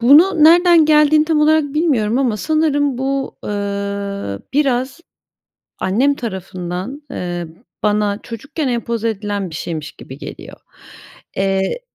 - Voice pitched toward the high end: Yes, high, 240 Hz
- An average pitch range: No, wide, 6.9 semitones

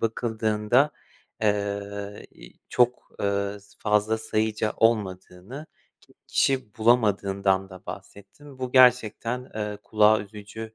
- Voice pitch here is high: No, low, 105 Hz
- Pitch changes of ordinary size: No, narrow, 2.3 semitones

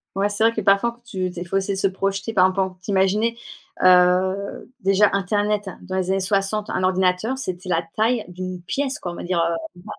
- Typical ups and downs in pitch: No, narrow, 2.2 semitones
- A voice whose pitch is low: No, high, 195 Hz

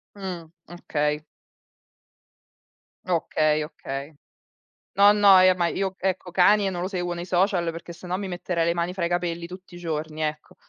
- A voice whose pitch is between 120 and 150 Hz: No, medium, 175 Hz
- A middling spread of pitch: No, narrow, 2.0 semitones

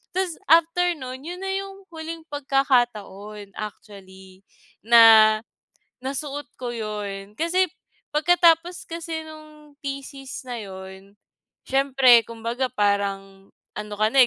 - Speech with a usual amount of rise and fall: No, wide, 7.0 semitones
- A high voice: Yes, very high, 255 Hz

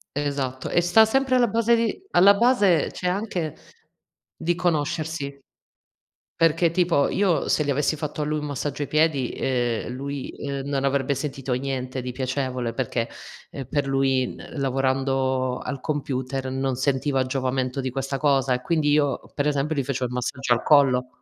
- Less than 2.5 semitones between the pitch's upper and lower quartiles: No, average, 2.8 semitones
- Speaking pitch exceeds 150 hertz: No, medium, 140 Hz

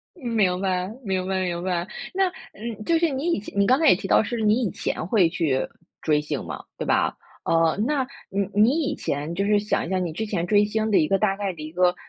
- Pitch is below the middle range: No, high, 195 Hz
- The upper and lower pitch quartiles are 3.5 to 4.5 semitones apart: Yes, average, 3.8 semitones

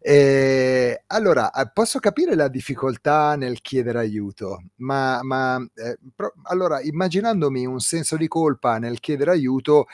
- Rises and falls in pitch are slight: No, average, 3.8 semitones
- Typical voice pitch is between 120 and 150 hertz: Yes, low, 135 Hz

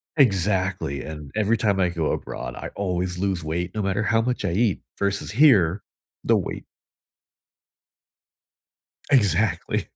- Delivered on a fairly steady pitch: No, average, 3.4 semitones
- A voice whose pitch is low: Yes, very low, 95 Hz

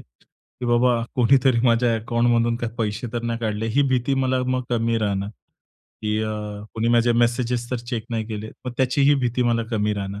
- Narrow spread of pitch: Yes, narrow, 1.8 semitones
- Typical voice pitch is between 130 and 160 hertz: No, low, 115 Hz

